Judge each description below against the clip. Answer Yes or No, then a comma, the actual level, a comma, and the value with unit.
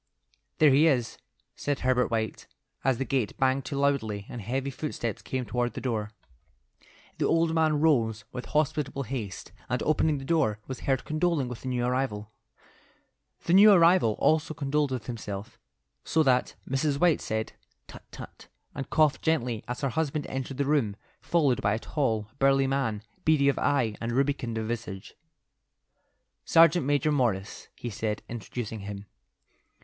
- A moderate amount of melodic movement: Yes, average, 4.5 semitones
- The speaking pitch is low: Yes, low, 130 Hz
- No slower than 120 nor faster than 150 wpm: No, average, 160 wpm